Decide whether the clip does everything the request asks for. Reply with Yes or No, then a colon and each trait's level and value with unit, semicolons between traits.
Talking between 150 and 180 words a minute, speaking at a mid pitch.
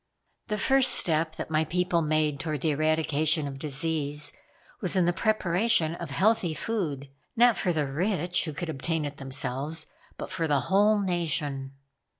Yes: average, 160 wpm; medium, 160 Hz